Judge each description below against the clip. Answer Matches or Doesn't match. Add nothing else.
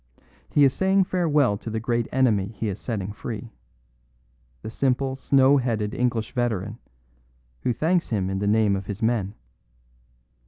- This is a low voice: Matches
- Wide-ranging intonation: Doesn't match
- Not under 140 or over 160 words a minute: Matches